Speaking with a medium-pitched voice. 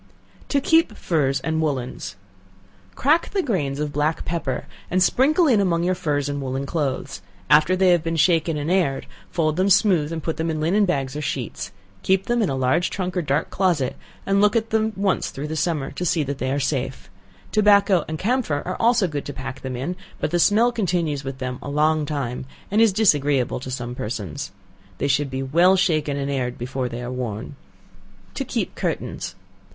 Yes: medium, 155 Hz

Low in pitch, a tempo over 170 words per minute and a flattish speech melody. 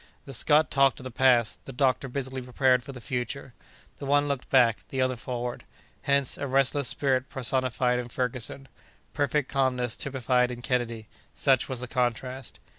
No: low, 130 Hz; average, 165 wpm; narrow, 1.7 semitones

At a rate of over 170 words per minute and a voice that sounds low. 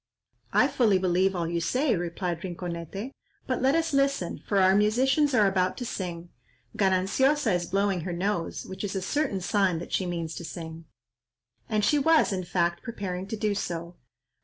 No: average, 180 wpm; high, 190 Hz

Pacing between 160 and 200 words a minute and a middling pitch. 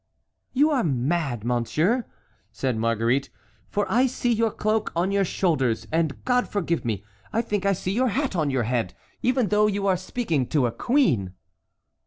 Yes: average, 175 wpm; medium, 180 Hz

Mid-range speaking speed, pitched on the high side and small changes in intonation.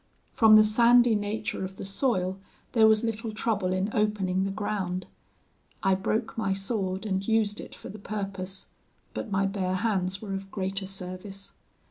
Yes: average, 165 wpm; high, 195 Hz; narrow, 2.1 semitones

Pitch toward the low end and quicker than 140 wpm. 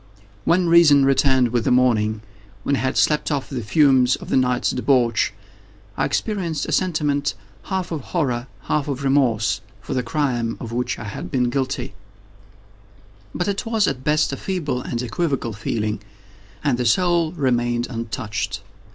Yes: low, 130 Hz; average, 155 wpm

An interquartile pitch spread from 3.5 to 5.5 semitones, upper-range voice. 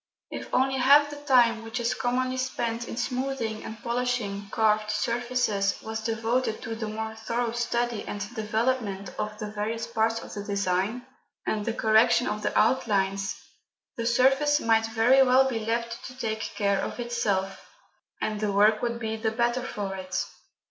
No: narrow, 2.5 semitones; high, 225 Hz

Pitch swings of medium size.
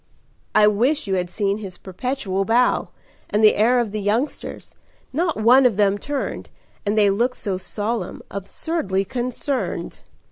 Yes: average, 4.1 semitones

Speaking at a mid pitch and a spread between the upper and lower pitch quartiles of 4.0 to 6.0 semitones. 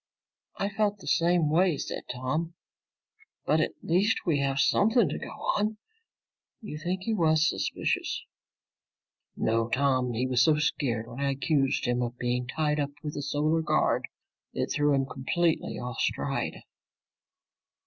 Yes: medium, 150 Hz; average, 4.7 semitones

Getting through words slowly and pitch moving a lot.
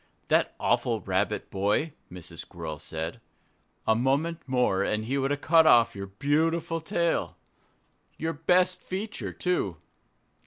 Yes: slow, 130 wpm; wide, 8.4 semitones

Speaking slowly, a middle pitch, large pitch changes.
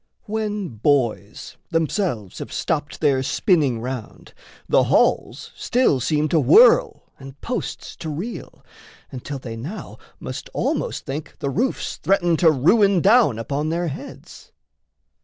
Yes: slow, 130 wpm; medium, 155 Hz; wide, 6.7 semitones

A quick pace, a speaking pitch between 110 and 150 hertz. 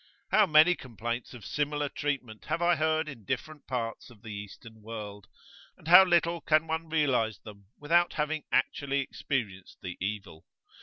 No: average, 160 wpm; low, 135 Hz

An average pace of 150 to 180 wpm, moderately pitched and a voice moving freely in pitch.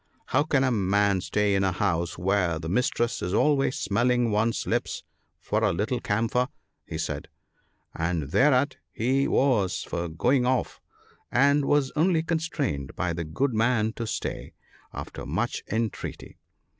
No: average, 155 wpm; low, 115 Hz; wide, 5.8 semitones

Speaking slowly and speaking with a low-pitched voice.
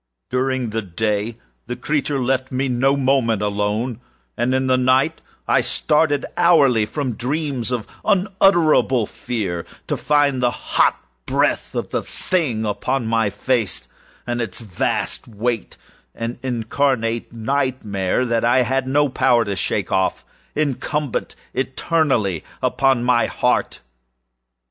Yes: slow, 125 wpm; low, 125 Hz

